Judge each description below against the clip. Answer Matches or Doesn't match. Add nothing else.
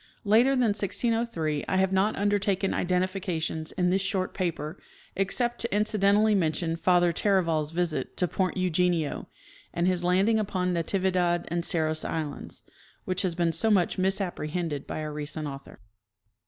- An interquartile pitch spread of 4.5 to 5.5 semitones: Doesn't match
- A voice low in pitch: Doesn't match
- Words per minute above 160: Doesn't match